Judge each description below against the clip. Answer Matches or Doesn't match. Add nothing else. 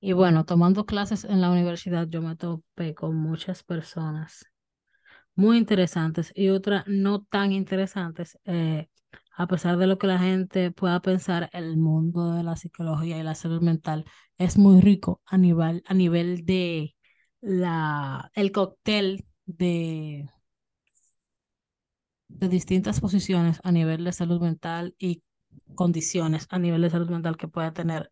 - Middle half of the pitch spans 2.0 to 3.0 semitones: Matches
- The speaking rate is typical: Matches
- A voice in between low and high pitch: Matches